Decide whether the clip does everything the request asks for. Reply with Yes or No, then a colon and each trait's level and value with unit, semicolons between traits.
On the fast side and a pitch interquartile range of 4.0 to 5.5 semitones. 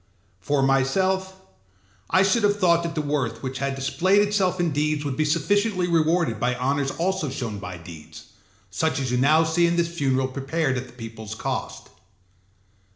No: average, 175 wpm; average, 4.9 semitones